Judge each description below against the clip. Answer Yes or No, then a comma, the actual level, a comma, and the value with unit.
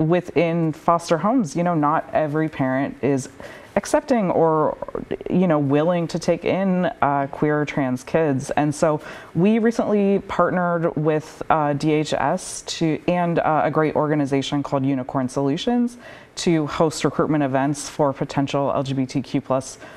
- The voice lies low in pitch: No, medium, 155 Hz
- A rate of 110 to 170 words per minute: Yes, average, 140 wpm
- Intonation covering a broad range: No, average, 3.7 semitones